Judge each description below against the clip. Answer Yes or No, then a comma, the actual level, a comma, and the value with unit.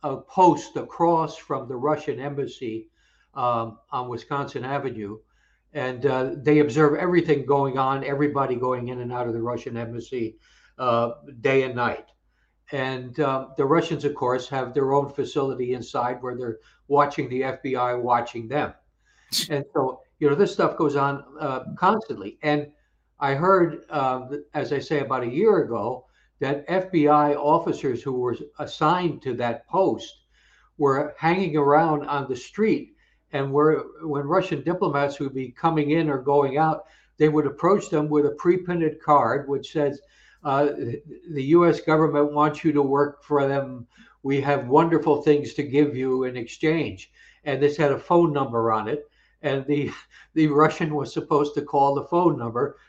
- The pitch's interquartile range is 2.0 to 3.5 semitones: Yes, average, 2.8 semitones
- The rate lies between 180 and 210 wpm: No, average, 165 wpm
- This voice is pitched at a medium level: Yes, medium, 145 Hz